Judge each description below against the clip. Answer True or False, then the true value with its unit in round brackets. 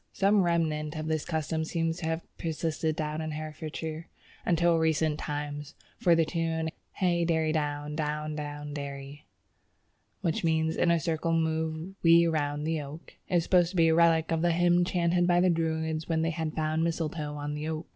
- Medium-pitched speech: True (160 Hz)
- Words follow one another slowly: False (180 wpm)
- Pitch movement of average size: False (1.5 semitones)